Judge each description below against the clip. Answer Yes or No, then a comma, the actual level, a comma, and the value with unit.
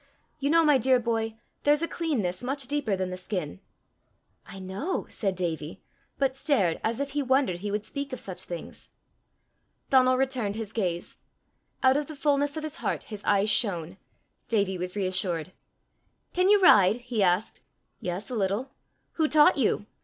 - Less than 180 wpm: Yes, average, 170 wpm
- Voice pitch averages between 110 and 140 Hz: No, high, 225 Hz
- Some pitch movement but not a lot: No, wide, 6.8 semitones